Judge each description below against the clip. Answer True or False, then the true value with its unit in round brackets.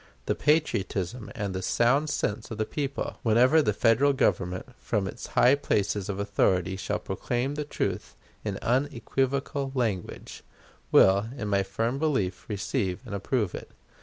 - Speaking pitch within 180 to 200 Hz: False (115 Hz)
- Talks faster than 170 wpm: False (150 wpm)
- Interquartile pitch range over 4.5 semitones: True (5.4 semitones)